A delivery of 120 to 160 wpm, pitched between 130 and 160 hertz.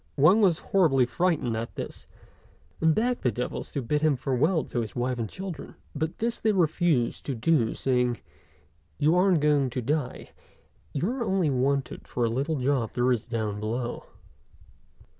No: average, 175 wpm; medium, 140 Hz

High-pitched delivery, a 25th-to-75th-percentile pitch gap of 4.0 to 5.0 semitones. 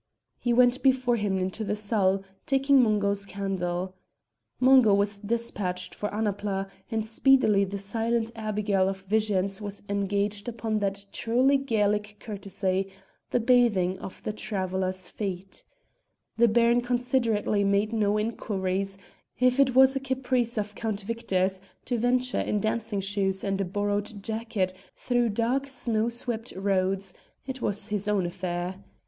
No: high, 210 Hz; average, 3.2 semitones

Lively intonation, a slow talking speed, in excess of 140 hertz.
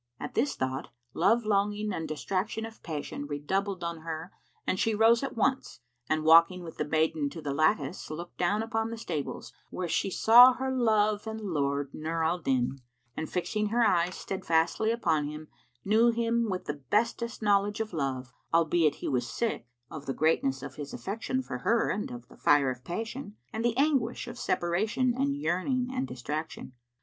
No: wide, 6.3 semitones; average, 180 wpm; medium, 185 Hz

